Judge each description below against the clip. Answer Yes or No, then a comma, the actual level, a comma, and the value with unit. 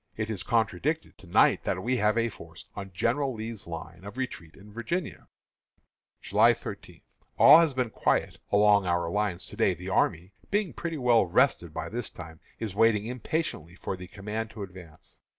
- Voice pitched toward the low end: Yes, low, 105 Hz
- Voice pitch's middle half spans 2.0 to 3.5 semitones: No, average, 4.5 semitones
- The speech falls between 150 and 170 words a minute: No, average, 180 wpm